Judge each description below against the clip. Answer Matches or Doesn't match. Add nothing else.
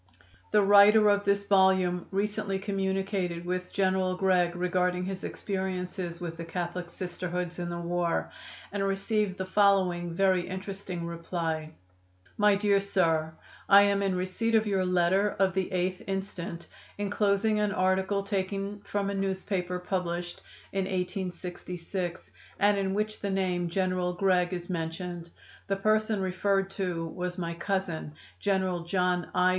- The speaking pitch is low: Doesn't match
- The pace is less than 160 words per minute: Matches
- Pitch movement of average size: Doesn't match